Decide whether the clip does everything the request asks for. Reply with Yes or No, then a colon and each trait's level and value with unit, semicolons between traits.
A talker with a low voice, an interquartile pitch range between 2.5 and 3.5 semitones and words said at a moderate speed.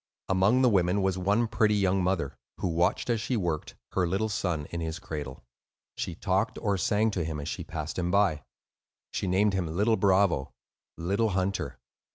Yes: very low, 95 Hz; average, 3.2 semitones; average, 185 wpm